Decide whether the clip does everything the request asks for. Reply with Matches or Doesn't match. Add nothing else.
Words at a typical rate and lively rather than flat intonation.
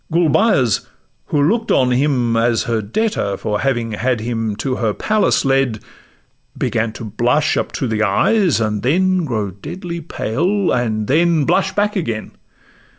Matches